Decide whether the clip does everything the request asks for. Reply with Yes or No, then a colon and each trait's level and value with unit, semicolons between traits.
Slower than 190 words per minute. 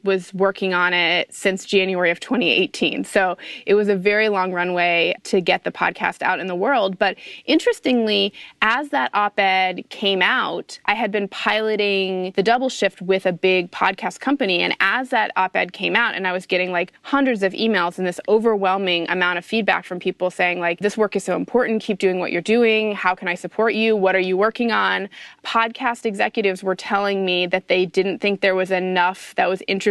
No: fast, 205 wpm